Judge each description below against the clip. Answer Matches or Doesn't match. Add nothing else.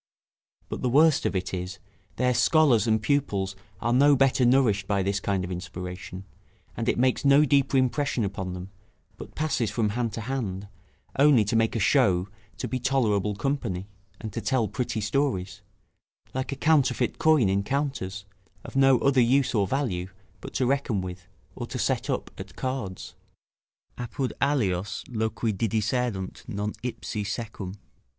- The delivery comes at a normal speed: Matches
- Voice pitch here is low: Matches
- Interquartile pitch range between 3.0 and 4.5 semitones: Doesn't match